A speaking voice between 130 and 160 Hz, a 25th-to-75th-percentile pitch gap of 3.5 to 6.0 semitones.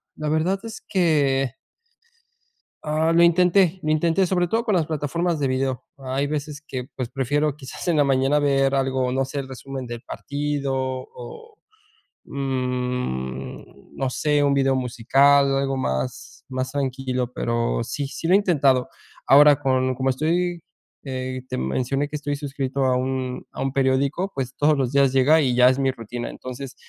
No: low, 135 Hz; narrow, 2.5 semitones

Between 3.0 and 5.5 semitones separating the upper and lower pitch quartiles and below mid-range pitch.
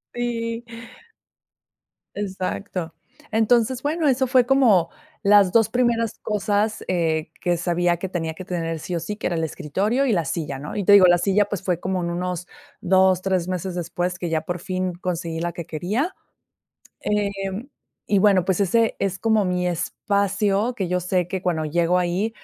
No: average, 3.3 semitones; medium, 185 Hz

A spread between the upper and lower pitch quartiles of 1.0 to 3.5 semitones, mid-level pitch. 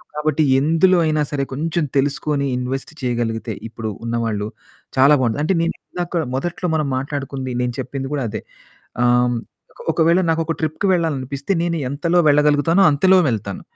No: average, 4.3 semitones; medium, 145 Hz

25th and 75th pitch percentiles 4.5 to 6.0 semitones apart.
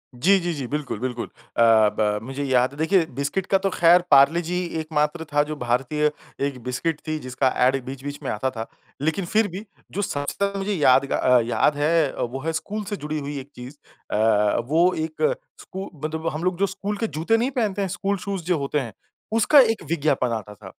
Yes: wide, 5.4 semitones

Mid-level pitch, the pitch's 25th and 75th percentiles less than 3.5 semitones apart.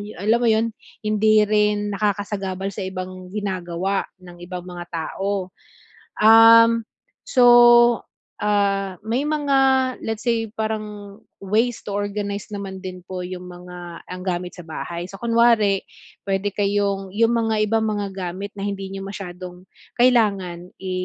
No: high, 200 Hz; average, 2.8 semitones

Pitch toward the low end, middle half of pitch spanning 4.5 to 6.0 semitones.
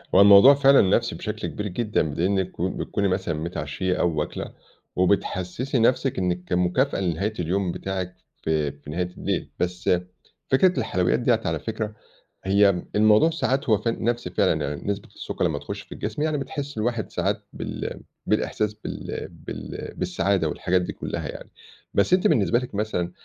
Yes: low, 100 Hz; average, 4.9 semitones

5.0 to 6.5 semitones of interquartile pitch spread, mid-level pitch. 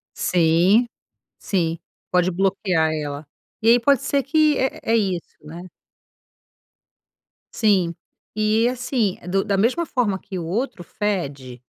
No: wide, 5.4 semitones; high, 195 Hz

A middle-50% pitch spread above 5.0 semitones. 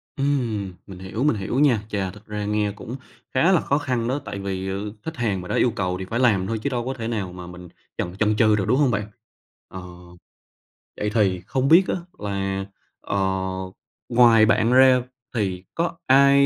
No: average, 4.7 semitones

